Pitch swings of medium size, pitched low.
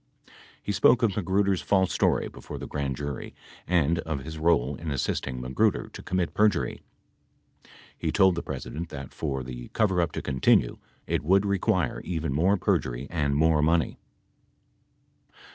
Yes: average, 5.0 semitones; very low, 80 Hz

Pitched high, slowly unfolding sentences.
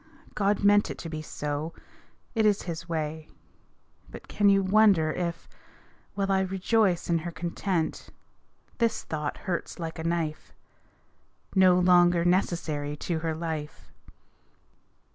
No: medium, 170 Hz; slow, 130 wpm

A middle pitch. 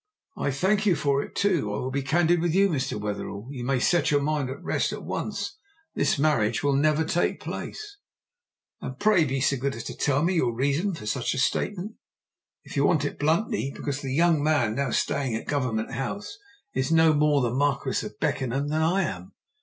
Yes: medium, 145 Hz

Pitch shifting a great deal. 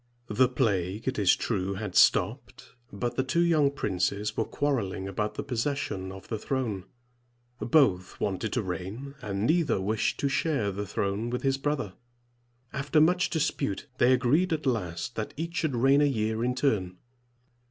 Yes: wide, 5.9 semitones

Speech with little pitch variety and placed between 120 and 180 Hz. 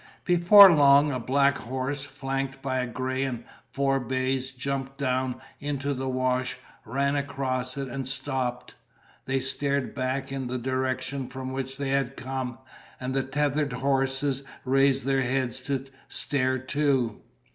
Yes: narrow, 1.2 semitones; low, 135 Hz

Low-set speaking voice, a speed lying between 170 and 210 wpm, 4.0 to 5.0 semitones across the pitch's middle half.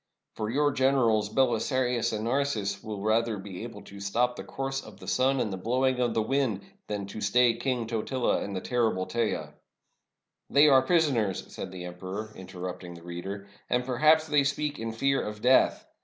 Yes: low, 115 Hz; average, 190 wpm; average, 4.6 semitones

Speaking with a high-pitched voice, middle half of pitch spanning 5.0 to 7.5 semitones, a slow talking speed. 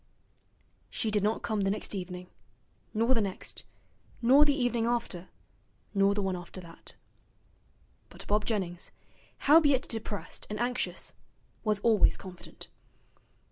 No: high, 210 Hz; average, 3.7 semitones; slow, 130 wpm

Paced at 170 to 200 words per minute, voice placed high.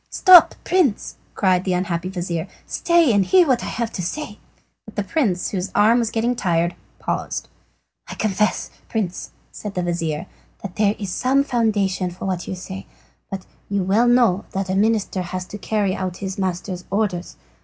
Yes: average, 175 wpm; high, 195 Hz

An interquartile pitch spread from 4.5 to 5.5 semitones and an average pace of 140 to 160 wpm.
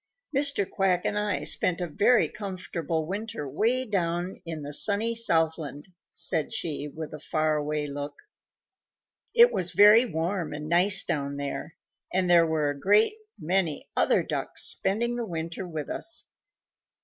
Yes: average, 4.9 semitones; average, 150 wpm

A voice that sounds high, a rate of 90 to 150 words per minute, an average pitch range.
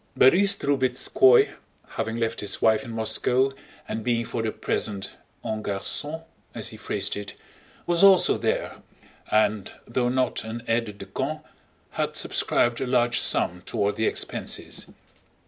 No: low, 115 Hz; average, 145 wpm; average, 3.3 semitones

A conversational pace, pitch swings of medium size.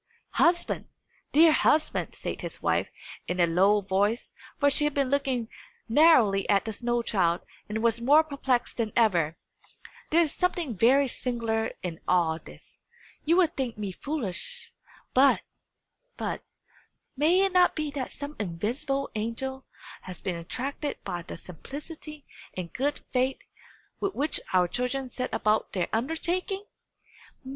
No: average, 145 wpm; wide, 6.4 semitones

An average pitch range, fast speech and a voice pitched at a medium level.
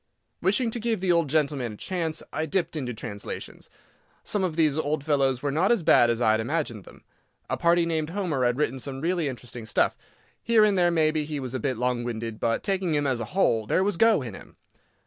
No: wide, 5.9 semitones; fast, 225 wpm; medium, 150 Hz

